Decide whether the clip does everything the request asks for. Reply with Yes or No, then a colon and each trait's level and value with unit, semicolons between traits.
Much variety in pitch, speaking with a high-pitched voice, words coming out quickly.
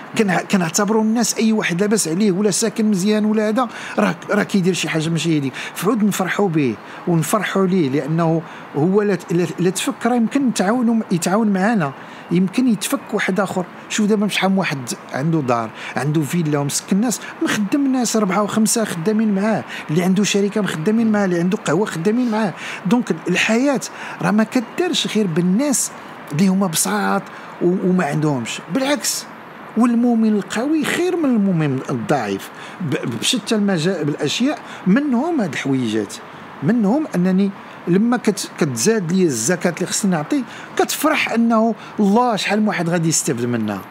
No: average, 4.1 semitones; high, 200 Hz; fast, 145 wpm